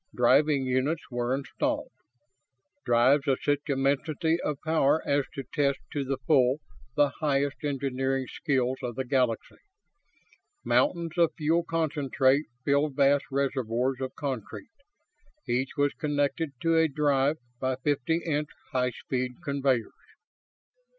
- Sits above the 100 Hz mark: Yes, medium, 140 Hz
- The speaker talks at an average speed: No, slow, 125 wpm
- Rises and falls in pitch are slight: Yes, narrow, 2.3 semitones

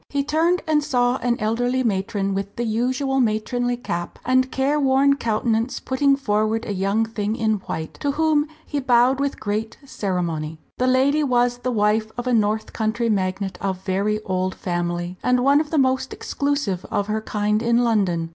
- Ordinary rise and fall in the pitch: Yes, average, 4.2 semitones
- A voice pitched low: No, high, 230 Hz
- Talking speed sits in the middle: Yes, average, 175 wpm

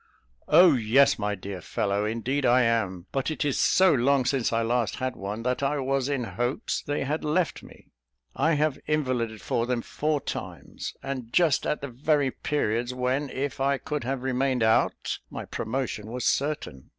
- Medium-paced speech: Yes, average, 180 wpm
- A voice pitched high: No, low, 130 Hz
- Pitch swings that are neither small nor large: Yes, average, 3.6 semitones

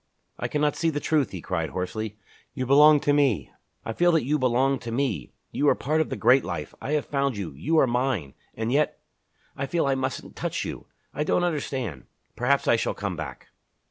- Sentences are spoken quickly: Yes, fast, 210 wpm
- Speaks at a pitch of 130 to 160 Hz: Yes, low, 135 Hz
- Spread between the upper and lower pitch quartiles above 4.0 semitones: Yes, average, 5.2 semitones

